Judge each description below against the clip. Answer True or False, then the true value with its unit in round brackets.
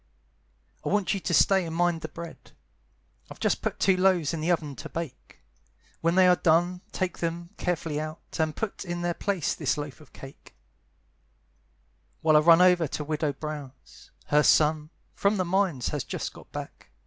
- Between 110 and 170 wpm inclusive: False (185 wpm)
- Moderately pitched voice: True (165 Hz)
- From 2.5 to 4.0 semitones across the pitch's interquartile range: True (2.8 semitones)